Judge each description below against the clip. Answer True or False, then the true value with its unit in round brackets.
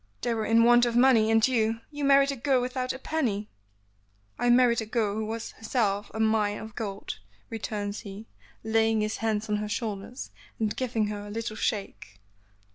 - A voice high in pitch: True (225 Hz)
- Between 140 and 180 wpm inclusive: False (195 wpm)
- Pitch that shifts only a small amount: True (2.3 semitones)